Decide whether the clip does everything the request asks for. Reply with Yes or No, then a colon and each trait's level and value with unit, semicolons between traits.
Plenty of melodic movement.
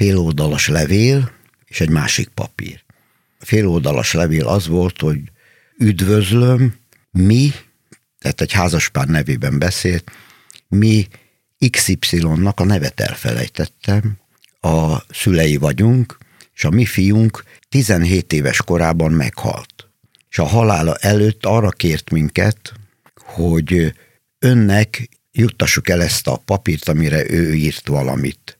Yes: wide, 5.8 semitones